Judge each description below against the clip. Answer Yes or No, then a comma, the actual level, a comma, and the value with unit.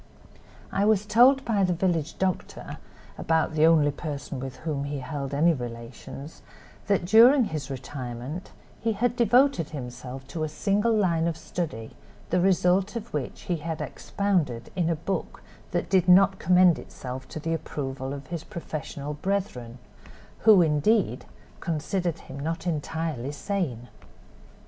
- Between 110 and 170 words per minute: Yes, average, 145 wpm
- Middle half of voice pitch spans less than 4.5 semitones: No, average, 5.2 semitones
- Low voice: No, medium, 165 Hz